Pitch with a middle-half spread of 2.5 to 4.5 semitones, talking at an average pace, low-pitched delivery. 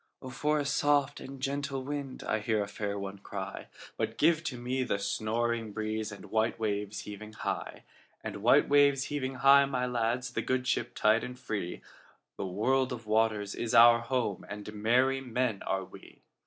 Yes: average, 3.8 semitones; average, 155 wpm; low, 120 Hz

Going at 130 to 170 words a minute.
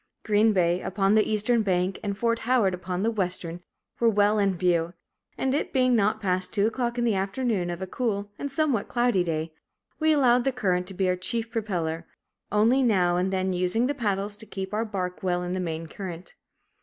No: fast, 205 wpm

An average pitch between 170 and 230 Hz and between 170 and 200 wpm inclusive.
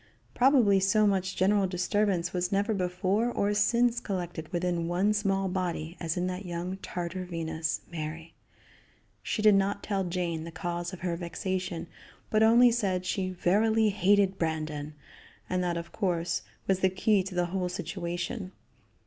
No: medium, 185 Hz; average, 155 wpm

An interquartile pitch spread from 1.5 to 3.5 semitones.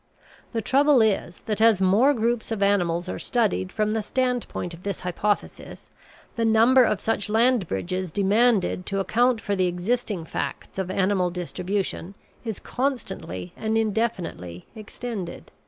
No: average, 3.9 semitones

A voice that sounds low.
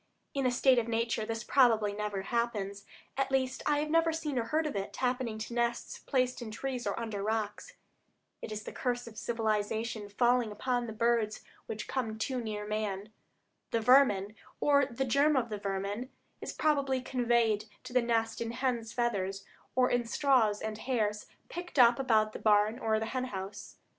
No: high, 230 Hz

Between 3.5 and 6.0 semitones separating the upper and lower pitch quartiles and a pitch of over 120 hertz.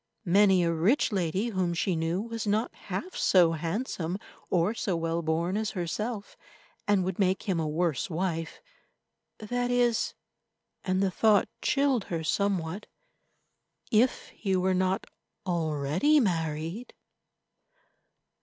Yes: average, 4.3 semitones; medium, 185 Hz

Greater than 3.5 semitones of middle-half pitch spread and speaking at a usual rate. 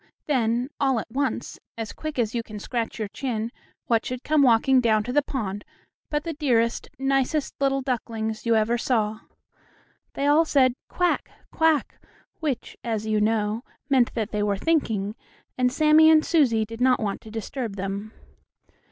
Yes: average, 4.0 semitones; average, 170 wpm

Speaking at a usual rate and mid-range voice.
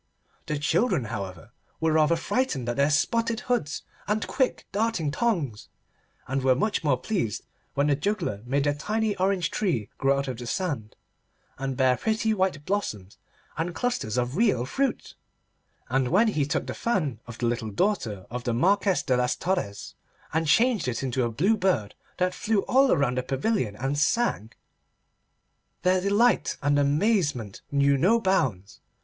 Yes: average, 165 wpm; medium, 150 Hz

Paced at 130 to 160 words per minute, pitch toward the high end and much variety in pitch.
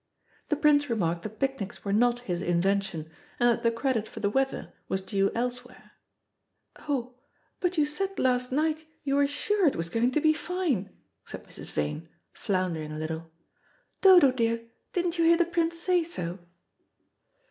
No: average, 170 wpm; high, 245 Hz; wide, 7.8 semitones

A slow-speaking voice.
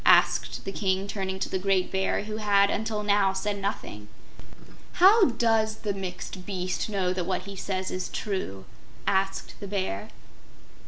No: average, 160 wpm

